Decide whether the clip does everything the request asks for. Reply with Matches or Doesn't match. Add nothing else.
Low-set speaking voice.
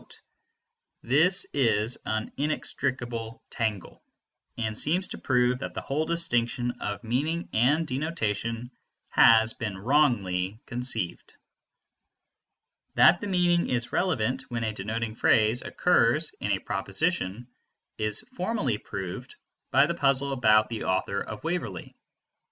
Matches